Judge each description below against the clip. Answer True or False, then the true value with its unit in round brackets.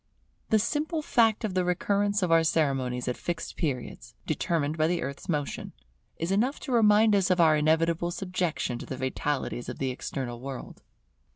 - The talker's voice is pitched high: False (165 Hz)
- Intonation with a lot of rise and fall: True (6.5 semitones)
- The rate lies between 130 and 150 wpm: False (175 wpm)